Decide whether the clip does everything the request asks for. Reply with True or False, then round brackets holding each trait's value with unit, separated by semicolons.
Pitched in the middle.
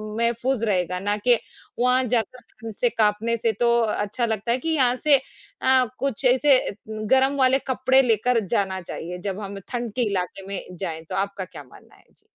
False (230 Hz)